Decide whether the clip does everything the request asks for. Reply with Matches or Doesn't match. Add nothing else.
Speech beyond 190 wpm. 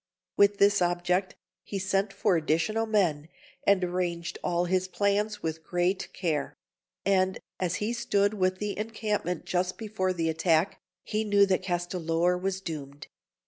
Doesn't match